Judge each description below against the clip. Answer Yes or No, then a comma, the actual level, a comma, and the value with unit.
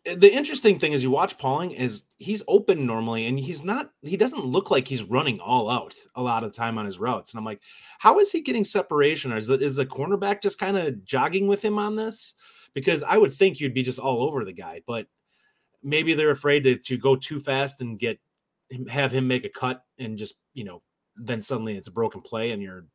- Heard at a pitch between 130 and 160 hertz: Yes, low, 135 Hz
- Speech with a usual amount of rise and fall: No, wide, 8.0 semitones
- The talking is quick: Yes, fast, 240 wpm